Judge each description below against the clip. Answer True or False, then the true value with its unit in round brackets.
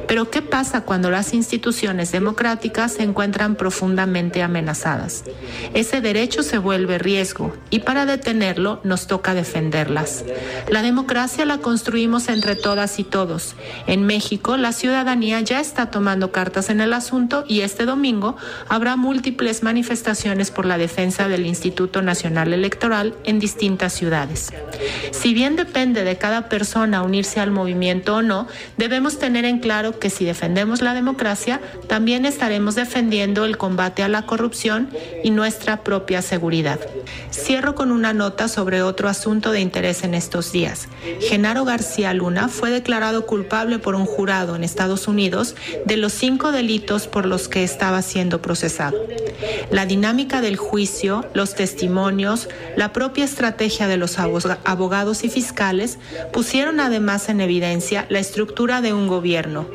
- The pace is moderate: True (145 wpm)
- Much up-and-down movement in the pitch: False (4.0 semitones)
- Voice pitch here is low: False (210 Hz)